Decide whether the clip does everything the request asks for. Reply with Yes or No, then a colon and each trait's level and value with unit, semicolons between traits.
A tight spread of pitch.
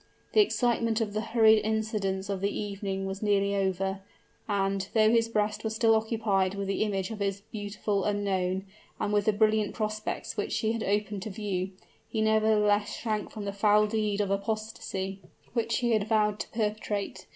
Yes: narrow, 1.6 semitones